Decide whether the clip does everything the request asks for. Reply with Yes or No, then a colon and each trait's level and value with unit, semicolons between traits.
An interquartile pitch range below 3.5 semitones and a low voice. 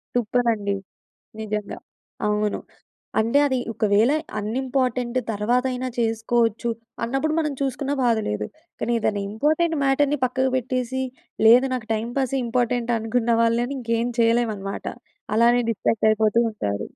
No: average, 2.7 semitones; high, 235 Hz